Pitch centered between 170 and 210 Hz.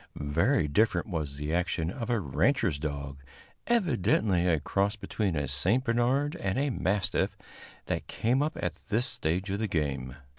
No: very low, 95 Hz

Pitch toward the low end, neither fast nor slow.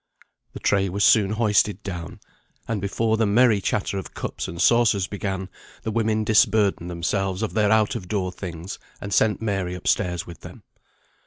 Yes: low, 100 Hz; average, 175 wpm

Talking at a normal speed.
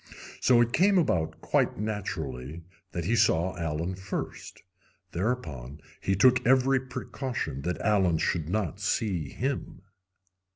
No: slow, 125 wpm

